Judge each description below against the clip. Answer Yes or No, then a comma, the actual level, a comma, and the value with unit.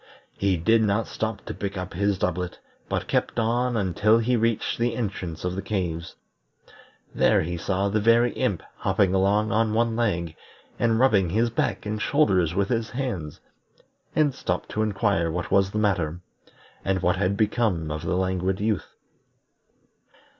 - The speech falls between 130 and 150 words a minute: No, average, 165 wpm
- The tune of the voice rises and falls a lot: No, average, 3.7 semitones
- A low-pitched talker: Yes, low, 100 Hz